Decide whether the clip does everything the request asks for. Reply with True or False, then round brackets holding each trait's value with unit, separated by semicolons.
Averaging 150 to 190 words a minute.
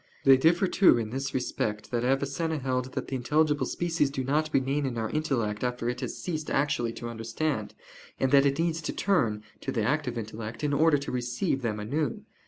False (200 wpm)